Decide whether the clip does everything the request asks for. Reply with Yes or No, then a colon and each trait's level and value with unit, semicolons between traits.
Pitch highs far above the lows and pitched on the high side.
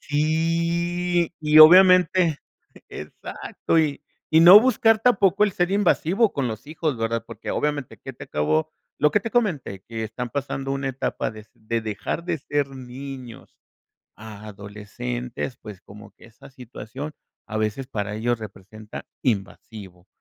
No: wide, 7.3 semitones; low, 135 Hz